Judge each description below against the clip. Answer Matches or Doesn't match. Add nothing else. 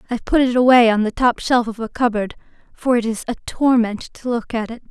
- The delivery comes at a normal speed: Doesn't match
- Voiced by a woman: Matches